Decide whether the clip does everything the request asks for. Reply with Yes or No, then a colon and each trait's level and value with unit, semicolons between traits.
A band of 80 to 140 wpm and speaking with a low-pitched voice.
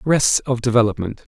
Yes: slow, 135 wpm; low, 120 Hz